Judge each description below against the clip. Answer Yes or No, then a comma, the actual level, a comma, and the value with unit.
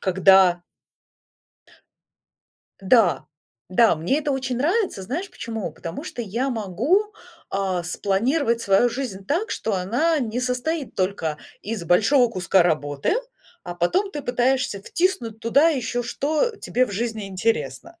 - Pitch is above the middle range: Yes, high, 230 Hz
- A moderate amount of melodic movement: No, wide, 6.2 semitones